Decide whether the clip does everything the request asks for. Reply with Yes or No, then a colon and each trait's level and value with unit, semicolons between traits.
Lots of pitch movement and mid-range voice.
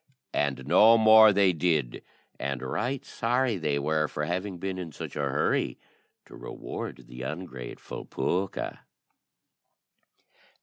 No: wide, 6.3 semitones; very low, 85 Hz